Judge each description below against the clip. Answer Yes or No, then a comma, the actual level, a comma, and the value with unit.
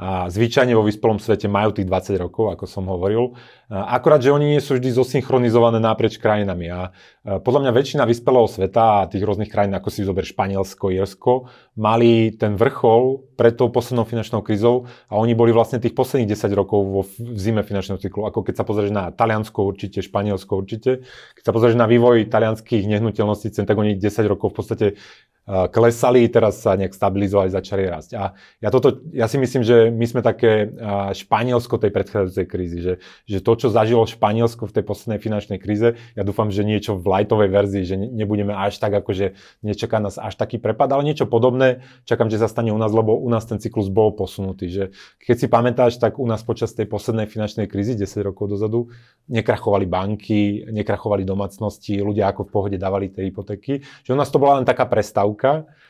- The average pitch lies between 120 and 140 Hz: No, low, 110 Hz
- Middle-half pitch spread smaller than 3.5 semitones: Yes, average, 2.8 semitones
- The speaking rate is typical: No, fast, 190 wpm